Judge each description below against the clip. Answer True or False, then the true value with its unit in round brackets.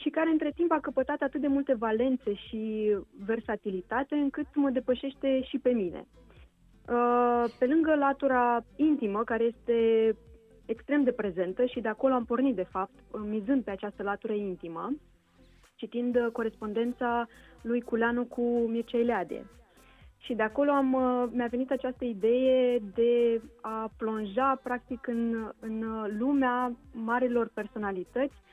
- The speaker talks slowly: False (135 wpm)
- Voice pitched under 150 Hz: False (240 Hz)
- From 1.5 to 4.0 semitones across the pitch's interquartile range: True (2.7 semitones)